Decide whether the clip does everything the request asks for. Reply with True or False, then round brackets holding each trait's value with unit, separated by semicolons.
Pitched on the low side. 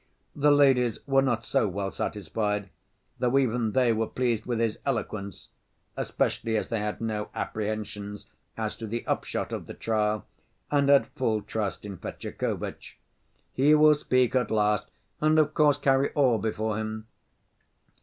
True (115 Hz)